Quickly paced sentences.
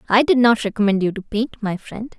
Yes: fast, 245 wpm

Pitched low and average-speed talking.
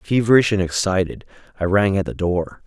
Yes: low, 100 Hz; average, 180 wpm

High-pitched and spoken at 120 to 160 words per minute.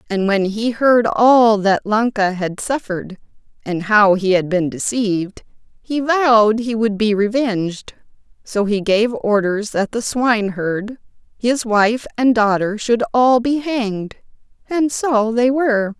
Yes: high, 220 Hz; average, 150 wpm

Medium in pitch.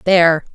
Yes: medium, 170 Hz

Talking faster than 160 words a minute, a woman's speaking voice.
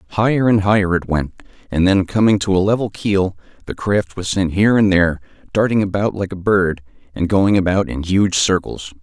No: average, 200 wpm; male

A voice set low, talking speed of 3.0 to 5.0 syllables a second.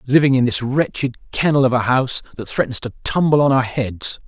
No: low, 130 Hz; 5.5 syllables/s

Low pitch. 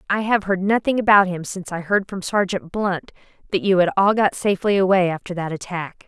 No: high, 190 Hz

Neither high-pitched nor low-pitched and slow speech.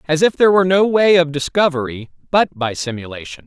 No: medium, 155 Hz; average, 190 wpm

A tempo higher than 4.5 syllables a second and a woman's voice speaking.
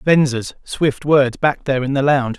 No: 5.0 syllables/s; male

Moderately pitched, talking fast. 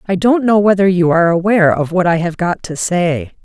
Yes: medium, 180 Hz; fast, 245 wpm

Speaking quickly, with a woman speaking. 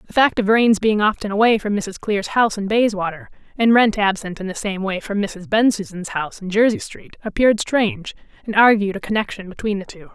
Yes: fast, 215 wpm; female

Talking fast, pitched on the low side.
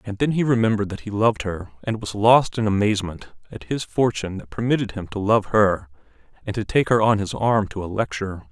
Yes: fast, 225 wpm; low, 105 Hz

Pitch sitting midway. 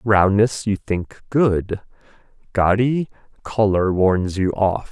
No: low, 100 Hz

